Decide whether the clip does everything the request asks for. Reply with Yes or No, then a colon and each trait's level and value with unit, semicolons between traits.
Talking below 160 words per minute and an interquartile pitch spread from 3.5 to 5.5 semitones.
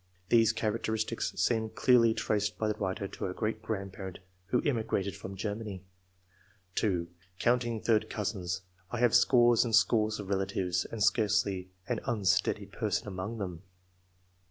No: average, 145 wpm; average, 2.9 semitones